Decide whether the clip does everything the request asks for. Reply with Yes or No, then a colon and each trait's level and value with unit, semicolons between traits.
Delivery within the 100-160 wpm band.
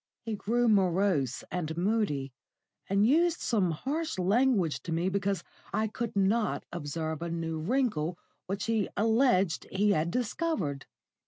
Yes: average, 140 wpm